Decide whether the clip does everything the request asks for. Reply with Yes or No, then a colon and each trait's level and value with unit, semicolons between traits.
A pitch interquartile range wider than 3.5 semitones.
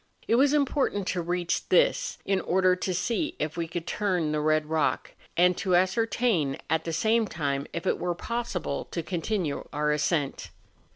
Yes: wide, 5.5 semitones